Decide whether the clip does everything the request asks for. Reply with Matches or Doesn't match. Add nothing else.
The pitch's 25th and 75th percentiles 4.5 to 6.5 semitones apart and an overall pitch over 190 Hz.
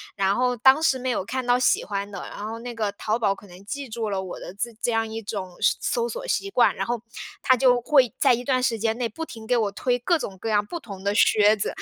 Doesn't match